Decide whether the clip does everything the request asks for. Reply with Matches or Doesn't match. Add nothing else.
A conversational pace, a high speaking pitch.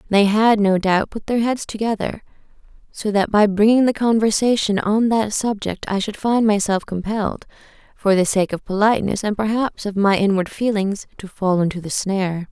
Matches